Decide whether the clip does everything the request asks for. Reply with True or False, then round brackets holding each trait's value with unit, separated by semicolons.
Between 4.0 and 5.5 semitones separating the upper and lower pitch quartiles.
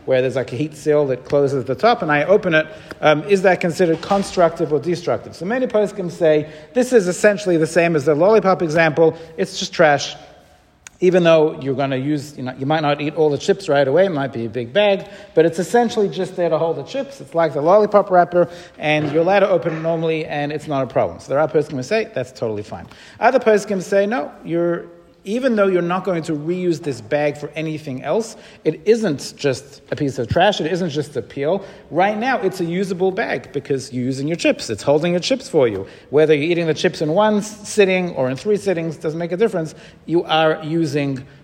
True (4.4 semitones)